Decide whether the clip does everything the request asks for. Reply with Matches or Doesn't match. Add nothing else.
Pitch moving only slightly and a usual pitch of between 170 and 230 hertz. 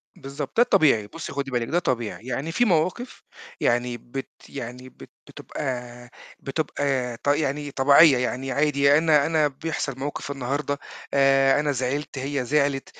Doesn't match